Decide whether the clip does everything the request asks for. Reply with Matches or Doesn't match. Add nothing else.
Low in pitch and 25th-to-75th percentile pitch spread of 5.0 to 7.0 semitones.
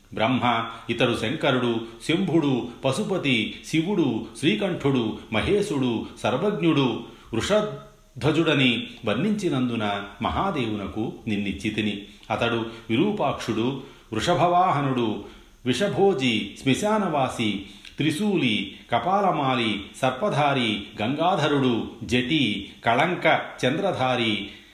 Matches